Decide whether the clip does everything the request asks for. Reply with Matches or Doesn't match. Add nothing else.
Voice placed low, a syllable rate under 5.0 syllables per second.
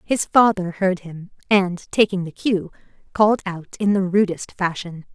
Doesn't match